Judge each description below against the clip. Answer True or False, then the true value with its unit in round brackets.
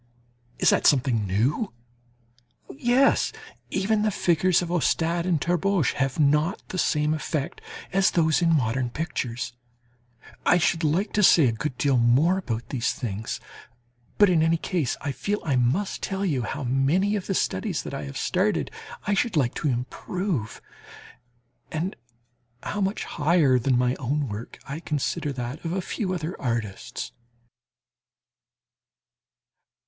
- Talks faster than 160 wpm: False (150 wpm)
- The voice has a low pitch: False (155 Hz)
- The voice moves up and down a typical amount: False (6.3 semitones)